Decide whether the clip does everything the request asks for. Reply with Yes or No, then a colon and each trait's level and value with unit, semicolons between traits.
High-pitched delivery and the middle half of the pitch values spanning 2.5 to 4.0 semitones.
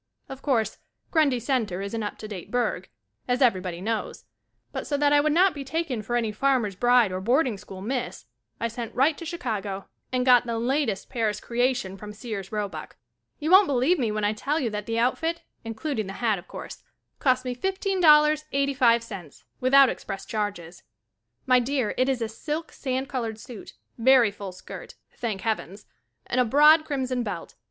No: high, 245 Hz; average, 4.6 semitones